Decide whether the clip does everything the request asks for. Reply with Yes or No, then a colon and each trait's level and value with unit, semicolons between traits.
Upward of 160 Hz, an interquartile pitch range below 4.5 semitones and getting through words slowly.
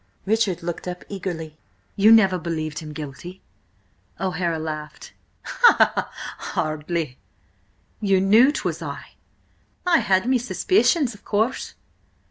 No: medium, 185 Hz; wide, 5.5 semitones; slow, 105 wpm